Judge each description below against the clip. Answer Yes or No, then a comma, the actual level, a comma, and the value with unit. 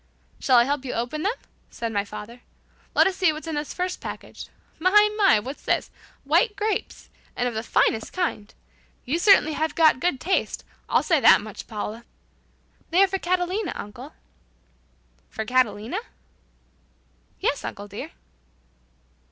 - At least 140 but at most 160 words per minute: Yes, average, 150 wpm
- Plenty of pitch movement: Yes, wide, 7.9 semitones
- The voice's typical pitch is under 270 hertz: No, very high, 300 Hz